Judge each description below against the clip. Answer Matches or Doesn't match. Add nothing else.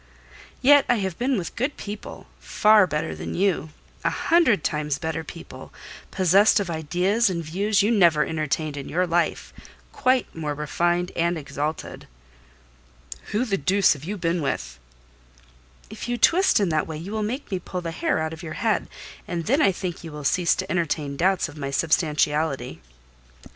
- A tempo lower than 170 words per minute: Doesn't match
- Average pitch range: Matches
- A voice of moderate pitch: Matches